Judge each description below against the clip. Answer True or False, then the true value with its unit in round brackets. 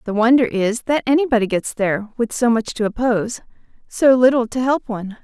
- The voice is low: False (235 Hz)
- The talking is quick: False (195 wpm)